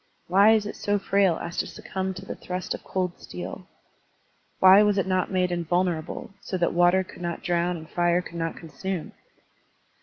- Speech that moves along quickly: No, average, 185 wpm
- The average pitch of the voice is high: No, medium, 180 Hz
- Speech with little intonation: Yes, narrow, 1.7 semitones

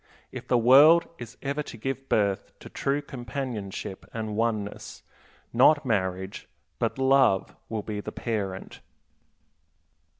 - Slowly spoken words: Yes, slow, 125 wpm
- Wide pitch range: No, average, 4.6 semitones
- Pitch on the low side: Yes, low, 115 Hz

